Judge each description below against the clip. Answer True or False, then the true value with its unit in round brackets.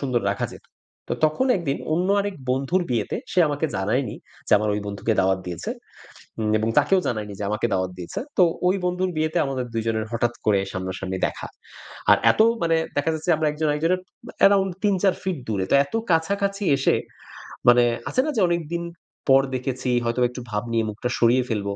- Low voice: True (130 Hz)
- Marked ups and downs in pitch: True (8.0 semitones)